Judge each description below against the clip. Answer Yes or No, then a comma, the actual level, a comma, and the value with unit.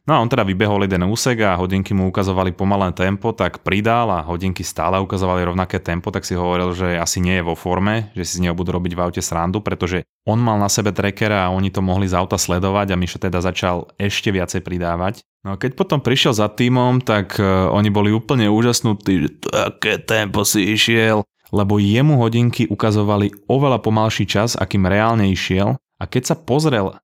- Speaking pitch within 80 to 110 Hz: Yes, low, 100 Hz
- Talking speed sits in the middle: No, fast, 200 wpm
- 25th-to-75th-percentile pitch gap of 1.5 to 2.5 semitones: No, average, 2.9 semitones